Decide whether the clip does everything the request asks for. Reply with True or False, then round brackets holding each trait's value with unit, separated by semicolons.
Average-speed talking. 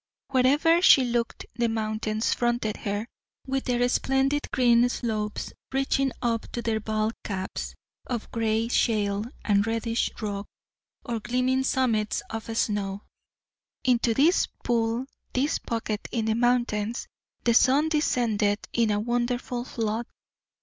False (130 wpm)